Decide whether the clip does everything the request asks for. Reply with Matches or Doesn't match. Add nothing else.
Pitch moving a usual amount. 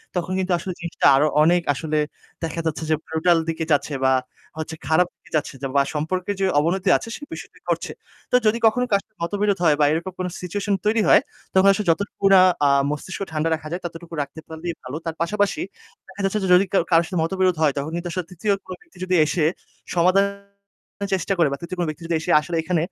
Matches